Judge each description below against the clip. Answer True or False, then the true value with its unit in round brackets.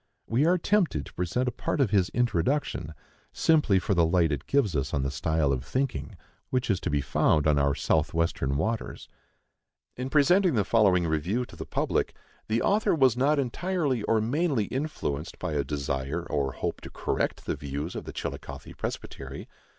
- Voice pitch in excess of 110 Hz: False (100 Hz)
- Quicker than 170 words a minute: True (185 wpm)